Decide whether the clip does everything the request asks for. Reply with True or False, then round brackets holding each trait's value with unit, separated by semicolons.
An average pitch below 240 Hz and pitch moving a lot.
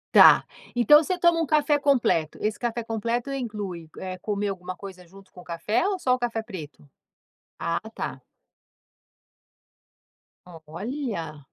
True (215 Hz; 6.0 semitones)